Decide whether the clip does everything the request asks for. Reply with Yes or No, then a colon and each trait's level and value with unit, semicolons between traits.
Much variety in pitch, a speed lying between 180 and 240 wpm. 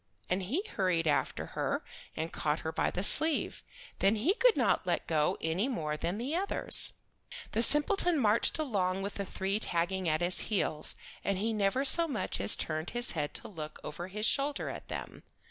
Yes: wide, 7.4 semitones; average, 190 wpm